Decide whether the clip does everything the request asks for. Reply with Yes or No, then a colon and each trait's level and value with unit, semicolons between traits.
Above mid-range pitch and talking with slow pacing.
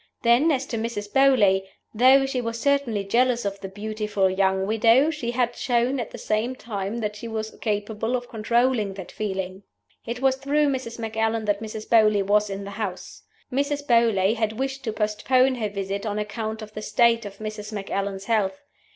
No: high, 220 Hz; average, 185 wpm